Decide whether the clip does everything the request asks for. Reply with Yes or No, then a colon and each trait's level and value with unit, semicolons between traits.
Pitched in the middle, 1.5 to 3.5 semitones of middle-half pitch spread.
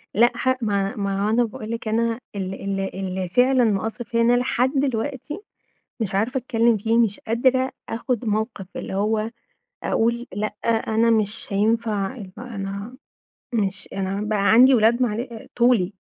No: high, 225 Hz; average, 3.0 semitones